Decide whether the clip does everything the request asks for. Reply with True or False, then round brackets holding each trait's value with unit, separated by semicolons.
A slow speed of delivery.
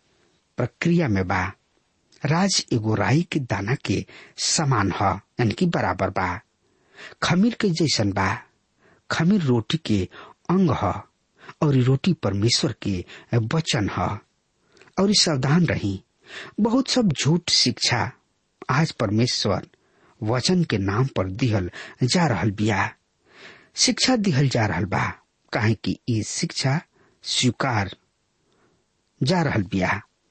True (105 wpm)